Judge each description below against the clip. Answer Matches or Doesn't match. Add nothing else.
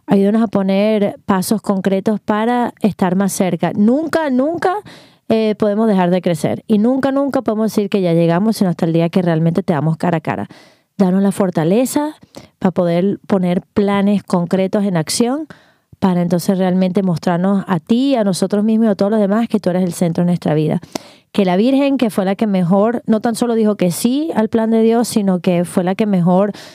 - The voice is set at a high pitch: Matches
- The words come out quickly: Matches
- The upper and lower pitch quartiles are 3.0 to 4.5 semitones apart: Matches